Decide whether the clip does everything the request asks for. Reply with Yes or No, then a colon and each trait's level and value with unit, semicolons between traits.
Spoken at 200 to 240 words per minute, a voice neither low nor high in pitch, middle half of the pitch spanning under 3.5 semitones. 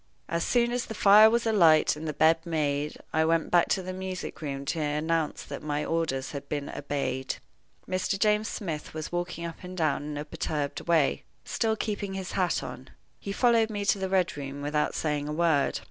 No: fast, 205 wpm; medium, 165 Hz; average, 4.4 semitones